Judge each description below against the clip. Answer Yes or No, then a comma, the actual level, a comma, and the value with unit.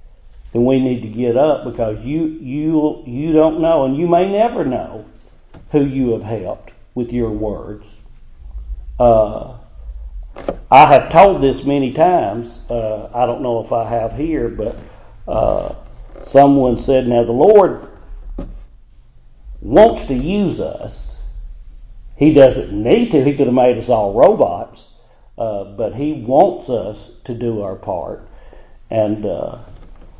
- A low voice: Yes, low, 120 Hz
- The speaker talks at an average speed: Yes, average, 145 wpm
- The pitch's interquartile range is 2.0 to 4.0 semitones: No, average, 4.4 semitones